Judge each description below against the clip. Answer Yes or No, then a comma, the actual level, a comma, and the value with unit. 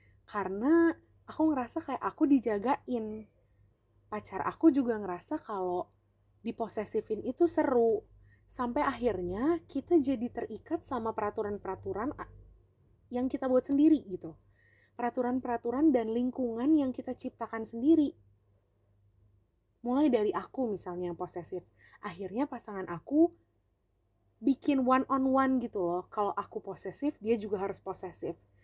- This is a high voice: Yes, high, 220 Hz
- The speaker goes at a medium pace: Yes, average, 115 wpm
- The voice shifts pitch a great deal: Yes, wide, 6.9 semitones